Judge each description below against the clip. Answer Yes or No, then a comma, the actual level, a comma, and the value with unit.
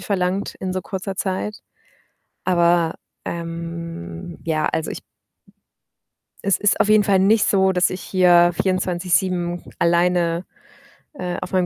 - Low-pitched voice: No, medium, 180 Hz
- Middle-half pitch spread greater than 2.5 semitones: No, narrow, 1.9 semitones